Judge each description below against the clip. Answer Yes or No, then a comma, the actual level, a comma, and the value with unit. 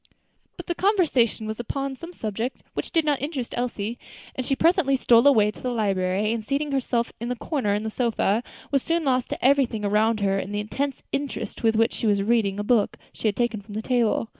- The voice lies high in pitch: Yes, high, 235 Hz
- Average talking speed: No, fast, 220 wpm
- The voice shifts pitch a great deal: No, average, 4.3 semitones